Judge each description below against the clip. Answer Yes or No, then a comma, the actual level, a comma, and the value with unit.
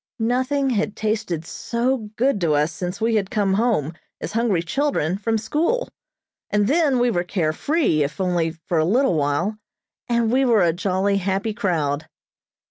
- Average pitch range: No, wide, 5.7 semitones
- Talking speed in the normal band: Yes, average, 170 wpm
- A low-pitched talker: No, high, 205 Hz